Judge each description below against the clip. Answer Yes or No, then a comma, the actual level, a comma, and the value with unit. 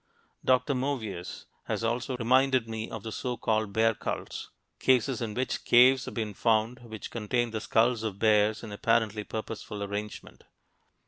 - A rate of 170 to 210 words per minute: No, average, 155 wpm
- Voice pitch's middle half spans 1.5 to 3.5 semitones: Yes, narrow, 2.4 semitones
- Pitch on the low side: Yes, low, 115 Hz